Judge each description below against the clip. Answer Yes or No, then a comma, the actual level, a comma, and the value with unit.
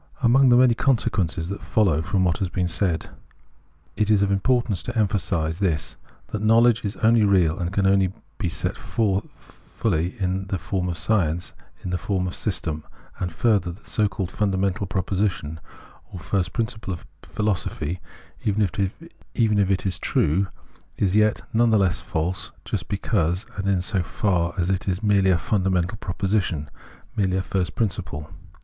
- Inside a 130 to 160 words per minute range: No, average, 175 wpm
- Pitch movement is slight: No, average, 3.0 semitones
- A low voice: Yes, very low, 95 Hz